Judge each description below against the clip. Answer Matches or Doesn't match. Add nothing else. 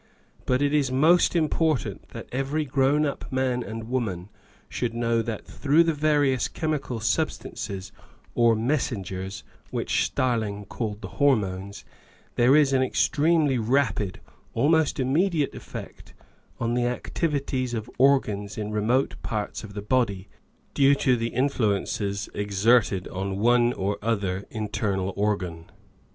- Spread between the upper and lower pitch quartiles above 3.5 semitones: Matches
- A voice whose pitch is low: Matches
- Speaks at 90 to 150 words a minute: Matches